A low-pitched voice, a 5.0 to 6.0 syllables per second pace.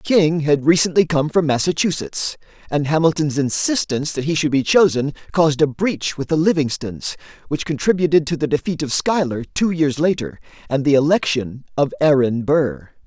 No: medium, 150 Hz; 5.1 syllables/s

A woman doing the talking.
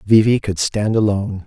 No: male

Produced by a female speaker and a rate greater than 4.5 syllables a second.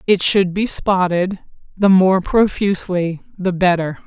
No: female; 4.1 syllables/s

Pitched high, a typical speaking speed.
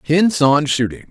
No: medium, 150 Hz; average, 165 wpm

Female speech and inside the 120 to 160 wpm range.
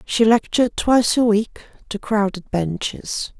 Yes: female; average, 140 wpm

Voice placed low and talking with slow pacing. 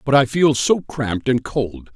No: low, 130 Hz; fast, 215 wpm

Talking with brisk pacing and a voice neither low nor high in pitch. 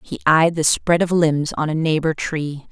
Yes: fast, 220 wpm; medium, 155 Hz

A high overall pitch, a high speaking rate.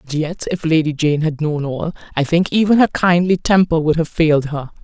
No: medium, 160 Hz; fast, 225 wpm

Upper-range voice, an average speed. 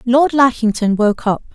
Yes: high, 240 Hz; average, 155 wpm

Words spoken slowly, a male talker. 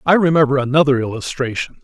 Yes: slow, 130 wpm; male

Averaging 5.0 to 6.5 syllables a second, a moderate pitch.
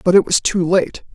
Yes: 5.1 syllables/s; medium, 180 Hz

